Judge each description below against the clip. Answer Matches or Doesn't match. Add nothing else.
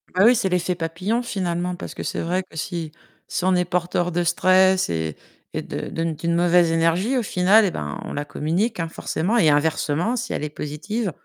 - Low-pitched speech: Doesn't match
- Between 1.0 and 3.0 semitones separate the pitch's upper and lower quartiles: Matches